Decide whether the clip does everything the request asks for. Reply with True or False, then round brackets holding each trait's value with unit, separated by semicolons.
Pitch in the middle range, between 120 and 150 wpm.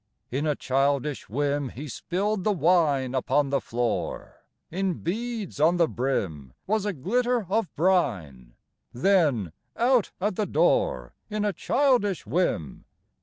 True (160 Hz; 135 wpm)